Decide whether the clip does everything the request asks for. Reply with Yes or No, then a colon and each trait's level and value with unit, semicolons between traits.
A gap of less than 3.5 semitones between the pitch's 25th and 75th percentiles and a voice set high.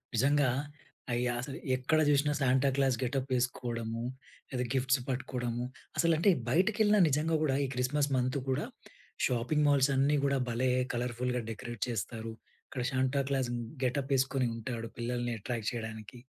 No: narrow, 2.5 semitones; low, 130 Hz